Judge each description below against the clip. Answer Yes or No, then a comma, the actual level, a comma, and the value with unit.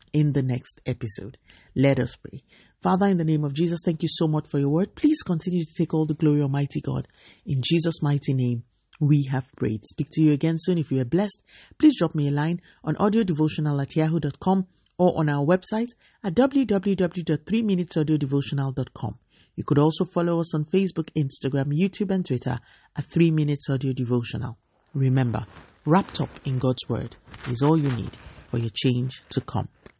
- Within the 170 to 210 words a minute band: Yes, average, 185 wpm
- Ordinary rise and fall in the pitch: Yes, average, 4.5 semitones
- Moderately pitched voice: Yes, medium, 150 Hz